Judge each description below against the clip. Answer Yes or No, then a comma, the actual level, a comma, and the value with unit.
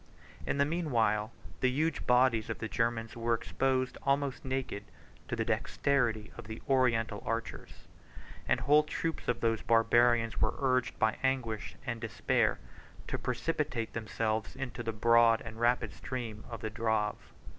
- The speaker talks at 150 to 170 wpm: Yes, average, 155 wpm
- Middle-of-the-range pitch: No, low, 115 Hz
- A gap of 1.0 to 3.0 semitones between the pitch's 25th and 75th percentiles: Yes, average, 2.7 semitones